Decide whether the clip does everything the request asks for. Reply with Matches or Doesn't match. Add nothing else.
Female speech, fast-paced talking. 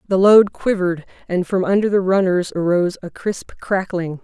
Doesn't match